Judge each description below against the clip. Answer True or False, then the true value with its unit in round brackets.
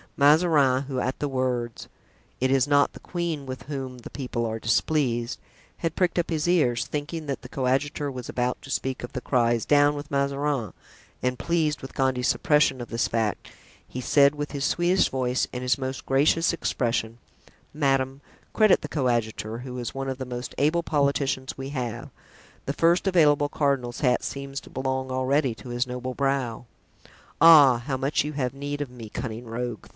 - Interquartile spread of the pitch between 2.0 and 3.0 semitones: True (2.7 semitones)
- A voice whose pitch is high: False (135 Hz)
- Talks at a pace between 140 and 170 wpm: False (180 wpm)